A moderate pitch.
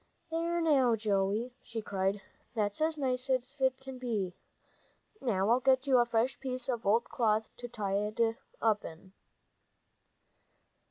No: high, 235 Hz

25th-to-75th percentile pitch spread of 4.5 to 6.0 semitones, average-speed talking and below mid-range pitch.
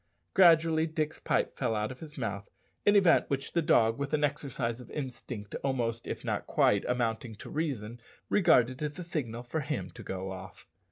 Yes: average, 5.1 semitones; average, 185 wpm; low, 130 Hz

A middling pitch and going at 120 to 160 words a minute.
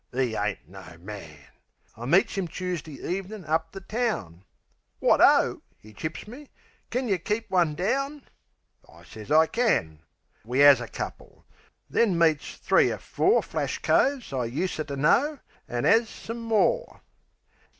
Yes: medium, 170 Hz; average, 150 wpm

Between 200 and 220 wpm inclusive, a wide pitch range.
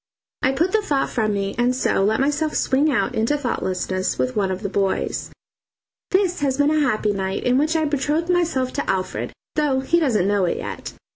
Yes: fast, 205 wpm; wide, 6.9 semitones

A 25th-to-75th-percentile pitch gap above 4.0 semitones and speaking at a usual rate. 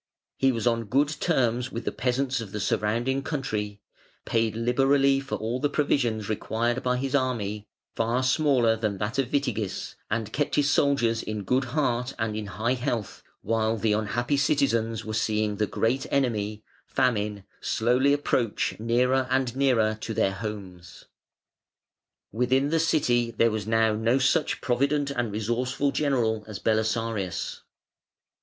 No: average, 3.5 semitones; average, 150 wpm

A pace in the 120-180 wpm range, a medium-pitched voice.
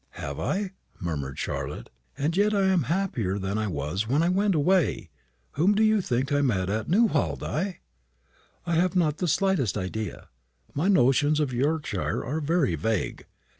Yes: average, 170 wpm; medium, 145 Hz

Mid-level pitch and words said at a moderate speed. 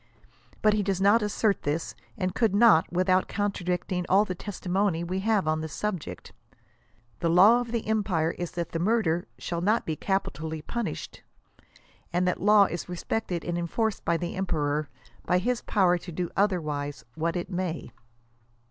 Yes: medium, 180 Hz; average, 165 wpm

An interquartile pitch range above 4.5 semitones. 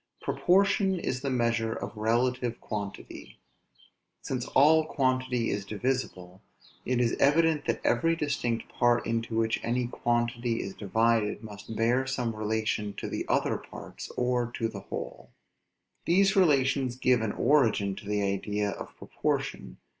No: average, 3.2 semitones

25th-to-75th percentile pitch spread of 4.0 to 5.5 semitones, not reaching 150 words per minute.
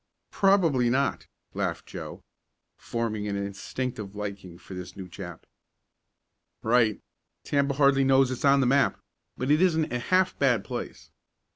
Yes: average, 5.2 semitones; average, 140 wpm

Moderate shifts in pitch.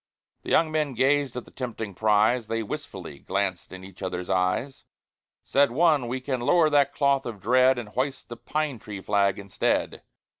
No: wide, 5.7 semitones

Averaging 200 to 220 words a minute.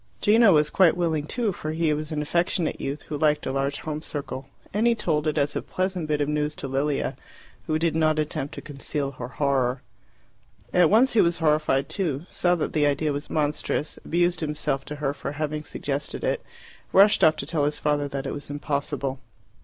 Yes: fast, 205 wpm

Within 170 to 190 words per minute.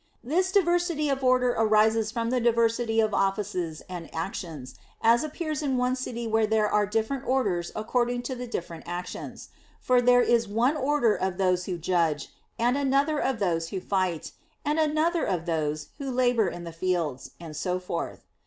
Yes: average, 175 wpm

